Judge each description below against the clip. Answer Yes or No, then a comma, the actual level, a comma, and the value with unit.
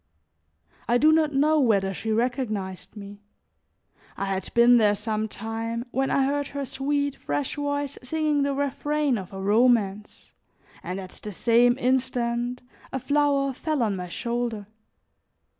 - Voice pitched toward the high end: Yes, high, 245 Hz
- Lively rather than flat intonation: No, average, 4.9 semitones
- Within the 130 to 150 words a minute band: Yes, average, 145 wpm